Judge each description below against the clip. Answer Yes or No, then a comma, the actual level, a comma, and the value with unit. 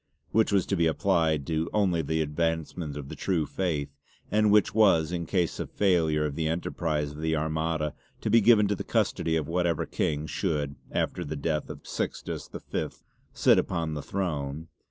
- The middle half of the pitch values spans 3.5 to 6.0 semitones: No, average, 2.9 semitones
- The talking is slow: No, average, 185 wpm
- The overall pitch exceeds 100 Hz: No, very low, 80 Hz